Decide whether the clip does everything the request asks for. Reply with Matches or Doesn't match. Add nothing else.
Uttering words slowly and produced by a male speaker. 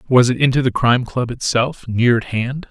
Doesn't match